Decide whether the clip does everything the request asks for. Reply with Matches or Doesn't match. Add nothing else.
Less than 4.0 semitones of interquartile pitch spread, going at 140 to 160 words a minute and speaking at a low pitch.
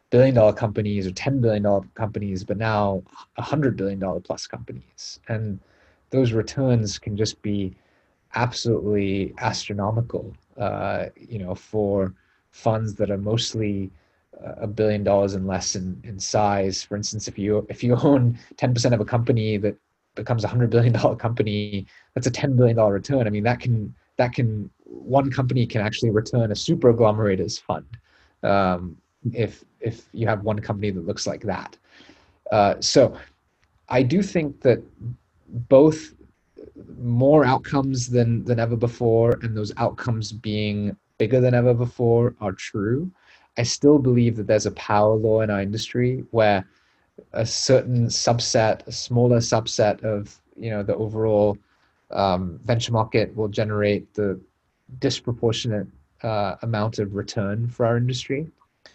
Matches